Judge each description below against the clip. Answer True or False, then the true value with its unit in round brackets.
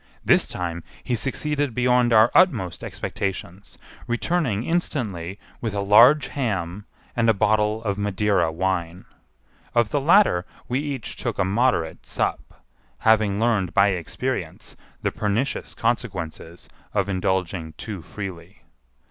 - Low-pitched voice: True (105 Hz)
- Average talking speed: False (125 wpm)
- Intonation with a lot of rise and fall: False (4.7 semitones)